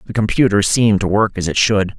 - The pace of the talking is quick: Yes, fast, 240 wpm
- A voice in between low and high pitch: No, low, 105 Hz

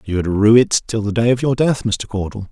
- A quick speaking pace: Yes, fast, 260 wpm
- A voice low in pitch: Yes, low, 110 Hz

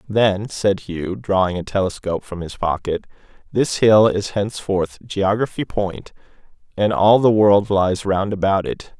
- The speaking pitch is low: Yes, low, 100 Hz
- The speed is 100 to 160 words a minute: Yes, average, 155 wpm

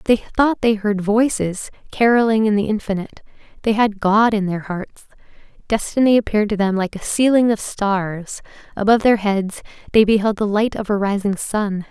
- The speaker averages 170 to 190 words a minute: Yes, average, 175 wpm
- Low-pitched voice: No, high, 210 Hz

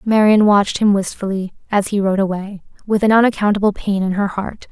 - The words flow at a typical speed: Yes, average, 190 wpm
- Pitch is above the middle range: Yes, high, 200 Hz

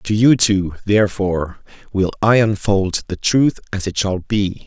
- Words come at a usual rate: Yes, average, 165 wpm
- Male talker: Yes, male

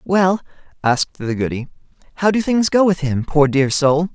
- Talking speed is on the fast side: No, average, 190 wpm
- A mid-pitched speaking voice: Yes, medium, 160 Hz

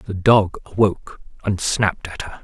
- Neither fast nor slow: Yes, average, 170 wpm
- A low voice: Yes, low, 100 Hz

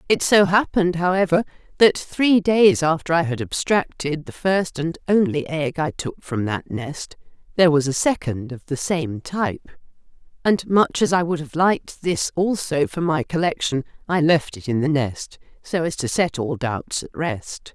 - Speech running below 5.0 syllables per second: Yes, 4.5 syllables/s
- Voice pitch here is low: No, medium, 160 Hz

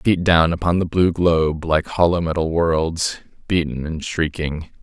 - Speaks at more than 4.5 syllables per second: No, 4.3 syllables/s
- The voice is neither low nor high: No, very low, 85 Hz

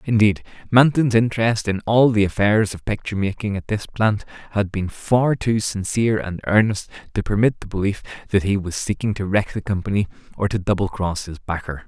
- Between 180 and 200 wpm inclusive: Yes, average, 190 wpm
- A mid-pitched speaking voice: No, low, 105 Hz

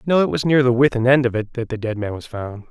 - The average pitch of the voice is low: Yes, low, 120 Hz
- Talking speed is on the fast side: Yes, fast, 335 wpm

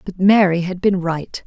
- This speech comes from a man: No, female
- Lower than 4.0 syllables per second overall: No, 4.4 syllables/s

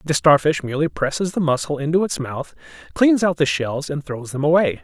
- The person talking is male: Yes, male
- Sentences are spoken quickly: Yes, fast, 210 wpm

